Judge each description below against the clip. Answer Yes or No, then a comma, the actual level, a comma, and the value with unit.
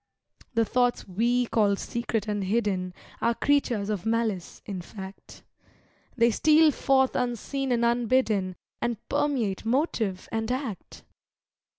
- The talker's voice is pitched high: Yes, high, 230 Hz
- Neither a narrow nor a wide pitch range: Yes, average, 3.6 semitones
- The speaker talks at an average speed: No, slow, 120 wpm